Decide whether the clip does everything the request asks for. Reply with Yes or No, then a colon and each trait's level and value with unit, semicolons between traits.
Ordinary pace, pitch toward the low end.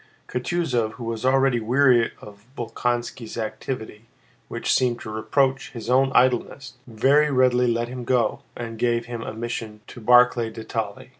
Yes: average, 155 wpm; low, 120 Hz